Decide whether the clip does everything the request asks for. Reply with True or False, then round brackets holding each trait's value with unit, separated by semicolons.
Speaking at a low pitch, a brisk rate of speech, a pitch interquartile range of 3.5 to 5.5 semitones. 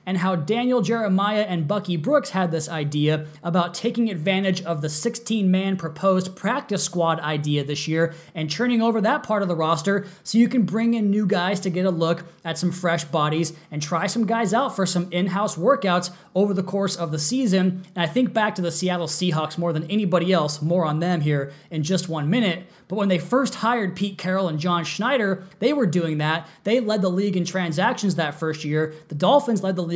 False (185 Hz; 215 wpm; 3.8 semitones)